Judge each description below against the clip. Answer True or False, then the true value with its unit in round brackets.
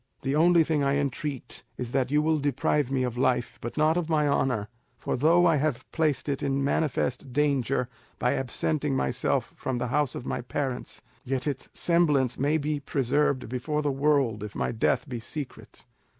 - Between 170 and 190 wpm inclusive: True (185 wpm)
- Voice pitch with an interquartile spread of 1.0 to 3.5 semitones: True (2.9 semitones)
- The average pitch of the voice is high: False (140 Hz)